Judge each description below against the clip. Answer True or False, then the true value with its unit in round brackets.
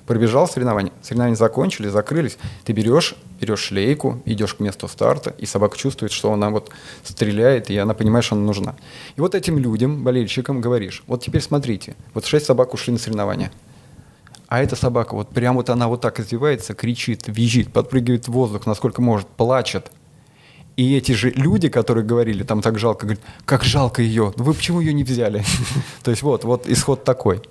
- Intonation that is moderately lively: True (3.5 semitones)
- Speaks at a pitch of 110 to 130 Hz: True (120 Hz)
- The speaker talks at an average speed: False (185 wpm)